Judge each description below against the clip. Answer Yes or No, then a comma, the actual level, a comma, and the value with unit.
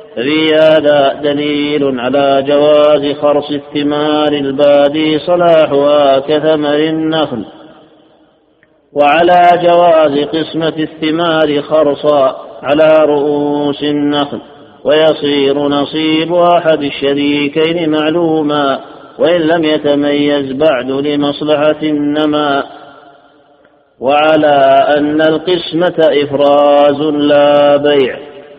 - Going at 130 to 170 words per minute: No, average, 75 wpm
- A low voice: No, medium, 150 Hz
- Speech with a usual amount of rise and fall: No, narrow, 1.4 semitones